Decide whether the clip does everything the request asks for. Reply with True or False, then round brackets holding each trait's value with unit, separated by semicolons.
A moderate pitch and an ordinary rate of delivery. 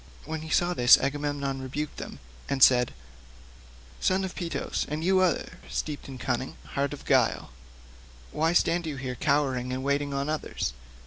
True (145 Hz; 165 wpm)